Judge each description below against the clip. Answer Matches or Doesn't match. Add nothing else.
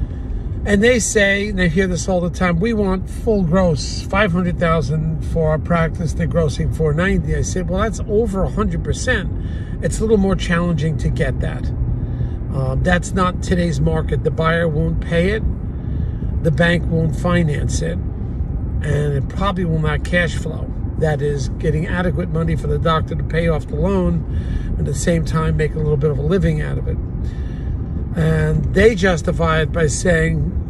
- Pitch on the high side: Doesn't match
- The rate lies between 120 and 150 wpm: Doesn't match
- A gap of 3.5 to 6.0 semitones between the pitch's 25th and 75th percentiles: Matches